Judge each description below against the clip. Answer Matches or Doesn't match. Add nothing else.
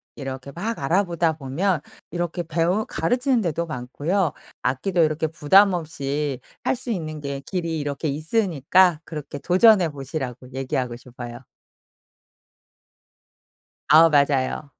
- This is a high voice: Doesn't match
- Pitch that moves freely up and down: Doesn't match